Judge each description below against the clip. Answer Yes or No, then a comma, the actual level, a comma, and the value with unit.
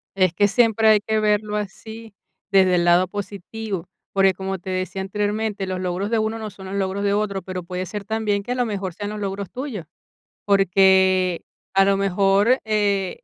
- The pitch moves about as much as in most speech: No, narrow, 2.0 semitones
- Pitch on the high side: Yes, high, 200 Hz